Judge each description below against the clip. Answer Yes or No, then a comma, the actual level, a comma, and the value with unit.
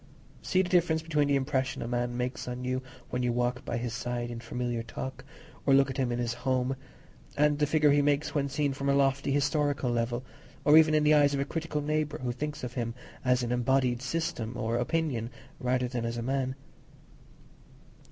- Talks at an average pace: No, fast, 210 wpm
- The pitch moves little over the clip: No, average, 3.1 semitones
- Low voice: Yes, low, 130 Hz